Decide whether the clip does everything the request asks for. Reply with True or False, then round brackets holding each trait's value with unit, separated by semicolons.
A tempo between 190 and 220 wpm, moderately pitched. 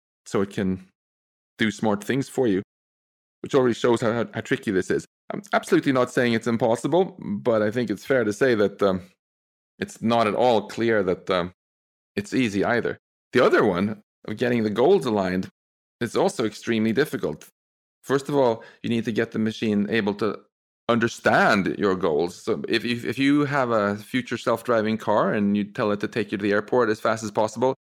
False (195 wpm; 110 Hz)